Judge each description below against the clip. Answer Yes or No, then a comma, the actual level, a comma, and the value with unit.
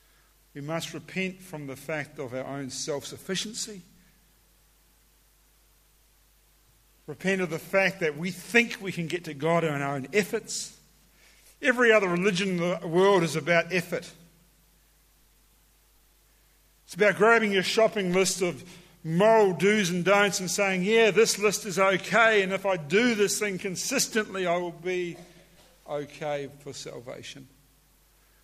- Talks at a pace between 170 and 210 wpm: No, average, 140 wpm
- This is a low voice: No, medium, 185 Hz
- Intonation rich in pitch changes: No, average, 3.5 semitones